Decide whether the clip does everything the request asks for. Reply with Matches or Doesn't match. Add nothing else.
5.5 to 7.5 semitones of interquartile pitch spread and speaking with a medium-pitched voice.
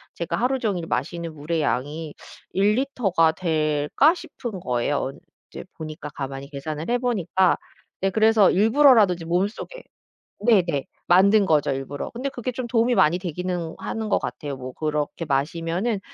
Matches